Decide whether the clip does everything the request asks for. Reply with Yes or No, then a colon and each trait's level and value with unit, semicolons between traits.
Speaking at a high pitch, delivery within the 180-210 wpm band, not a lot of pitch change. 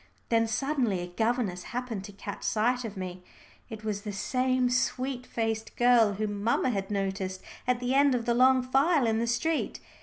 No: high, 230 Hz; average, 185 wpm; average, 3.6 semitones